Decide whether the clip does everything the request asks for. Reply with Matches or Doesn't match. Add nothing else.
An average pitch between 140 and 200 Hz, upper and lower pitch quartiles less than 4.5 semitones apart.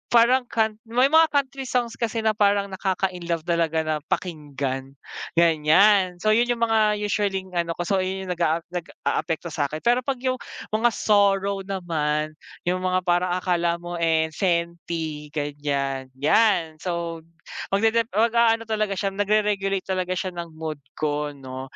Doesn't match